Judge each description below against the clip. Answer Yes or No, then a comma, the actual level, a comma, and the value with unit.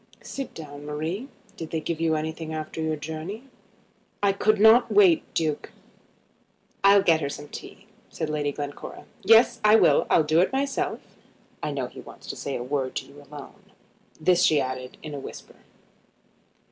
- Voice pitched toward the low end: No, medium, 160 Hz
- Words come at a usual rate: Yes, average, 170 wpm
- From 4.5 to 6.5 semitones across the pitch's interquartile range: Yes, wide, 5.4 semitones